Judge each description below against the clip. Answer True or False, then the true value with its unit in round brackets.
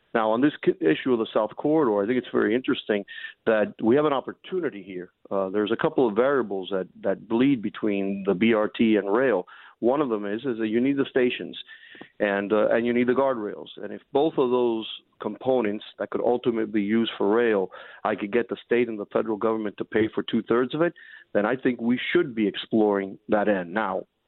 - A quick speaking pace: True (220 wpm)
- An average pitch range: True (3.2 semitones)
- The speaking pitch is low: True (115 Hz)